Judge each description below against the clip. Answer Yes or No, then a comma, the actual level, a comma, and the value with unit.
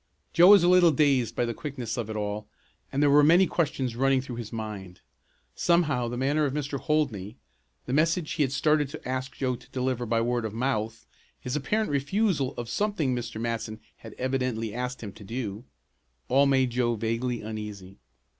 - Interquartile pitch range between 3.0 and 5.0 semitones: Yes, average, 4.1 semitones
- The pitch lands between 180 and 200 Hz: No, low, 125 Hz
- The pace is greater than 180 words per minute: Yes, average, 190 wpm